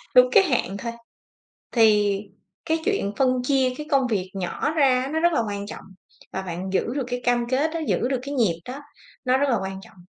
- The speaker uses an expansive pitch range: Yes, wide, 5.7 semitones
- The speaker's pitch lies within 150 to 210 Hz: No, very high, 250 Hz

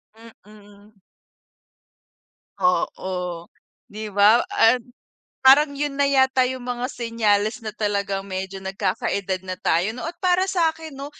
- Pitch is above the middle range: Yes, high, 215 Hz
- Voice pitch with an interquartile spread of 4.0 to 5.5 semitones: Yes, average, 5.1 semitones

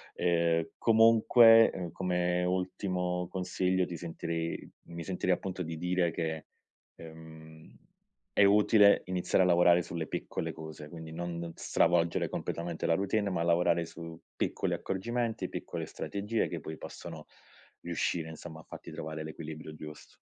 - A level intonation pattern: Yes, narrow, 2.2 semitones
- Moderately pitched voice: No, very low, 85 Hz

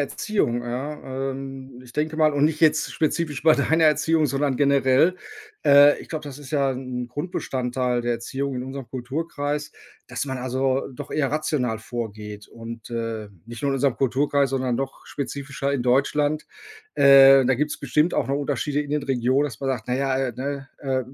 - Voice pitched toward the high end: No, low, 135 Hz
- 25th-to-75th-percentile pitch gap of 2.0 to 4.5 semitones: Yes, narrow, 2.5 semitones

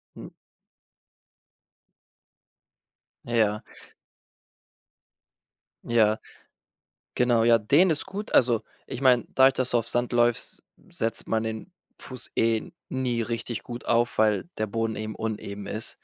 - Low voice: Yes, low, 115 Hz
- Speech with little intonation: Yes, narrow, 2.0 semitones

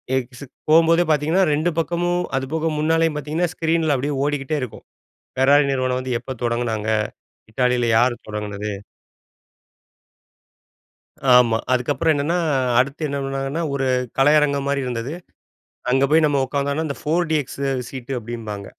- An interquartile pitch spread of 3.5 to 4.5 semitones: Yes, average, 3.8 semitones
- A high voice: No, medium, 140 Hz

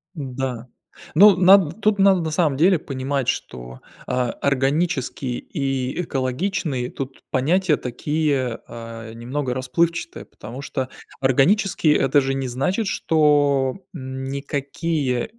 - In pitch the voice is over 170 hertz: No, low, 135 Hz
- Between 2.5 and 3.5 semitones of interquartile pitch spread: No, average, 4.2 semitones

